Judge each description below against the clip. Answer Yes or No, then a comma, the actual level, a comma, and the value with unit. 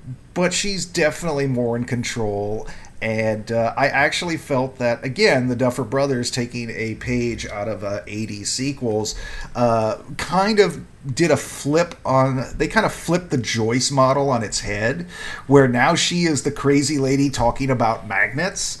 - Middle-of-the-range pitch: No, low, 130 Hz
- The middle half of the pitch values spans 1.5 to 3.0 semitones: No, average, 3.9 semitones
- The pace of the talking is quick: No, average, 165 wpm